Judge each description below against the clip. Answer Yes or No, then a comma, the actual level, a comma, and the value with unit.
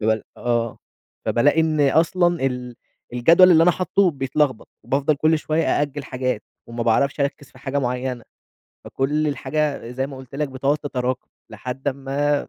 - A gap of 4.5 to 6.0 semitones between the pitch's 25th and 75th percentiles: No, average, 3.1 semitones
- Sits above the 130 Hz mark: Yes, medium, 140 Hz